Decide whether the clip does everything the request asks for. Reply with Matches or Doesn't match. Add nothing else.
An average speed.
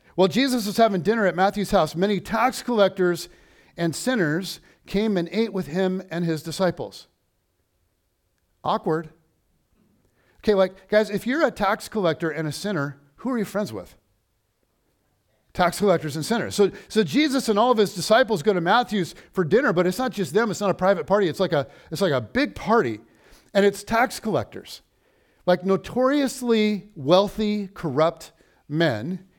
Matches